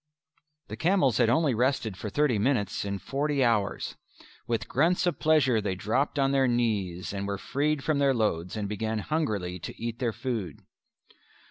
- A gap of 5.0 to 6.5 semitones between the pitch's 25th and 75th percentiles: Yes, wide, 5.4 semitones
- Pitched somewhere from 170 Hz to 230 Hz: No, low, 120 Hz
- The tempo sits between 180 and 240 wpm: No, average, 170 wpm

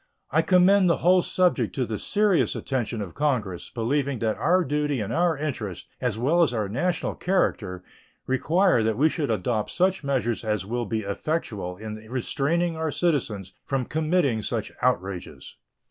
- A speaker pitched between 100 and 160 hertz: Yes, low, 135 Hz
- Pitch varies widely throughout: Yes, wide, 7.1 semitones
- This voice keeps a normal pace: Yes, average, 160 wpm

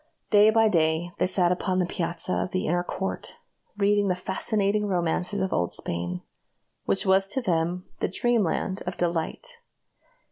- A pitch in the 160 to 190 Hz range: Yes, medium, 185 Hz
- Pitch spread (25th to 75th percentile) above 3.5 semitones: No, average, 2.9 semitones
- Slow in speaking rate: No, average, 155 wpm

